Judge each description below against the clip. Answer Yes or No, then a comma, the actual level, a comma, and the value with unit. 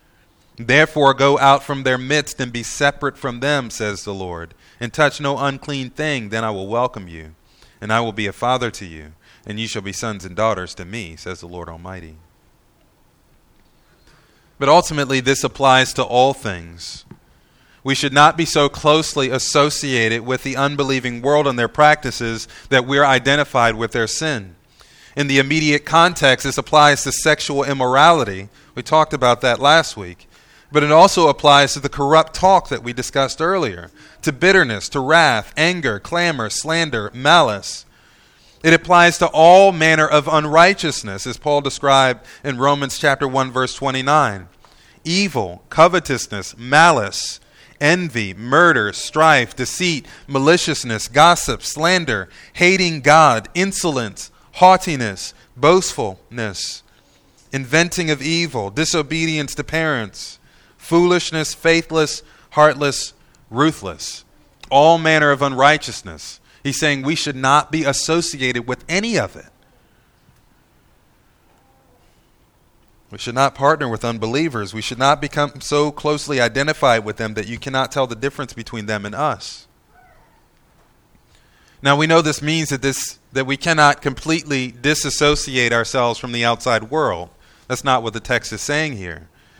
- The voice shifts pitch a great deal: No, average, 4.7 semitones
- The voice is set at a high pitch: No, medium, 140 Hz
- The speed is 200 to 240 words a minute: No, average, 145 wpm